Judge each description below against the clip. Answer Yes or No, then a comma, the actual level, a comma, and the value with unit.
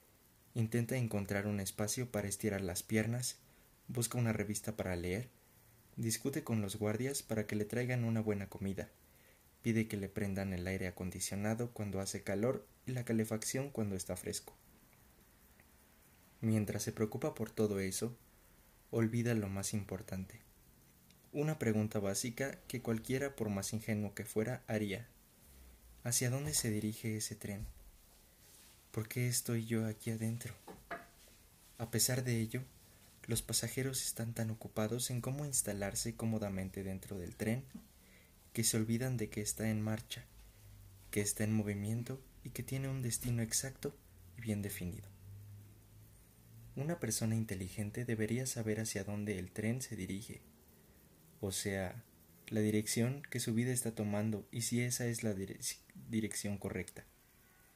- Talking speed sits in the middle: Yes, average, 145 wpm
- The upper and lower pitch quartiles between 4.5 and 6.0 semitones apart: No, average, 2.8 semitones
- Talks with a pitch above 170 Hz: No, low, 110 Hz